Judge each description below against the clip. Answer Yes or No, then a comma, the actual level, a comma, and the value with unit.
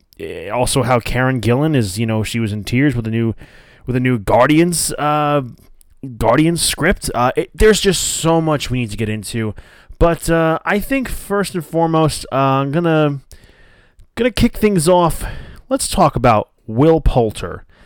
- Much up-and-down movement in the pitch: Yes, wide, 5.8 semitones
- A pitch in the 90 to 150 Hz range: Yes, medium, 140 Hz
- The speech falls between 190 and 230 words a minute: No, average, 170 wpm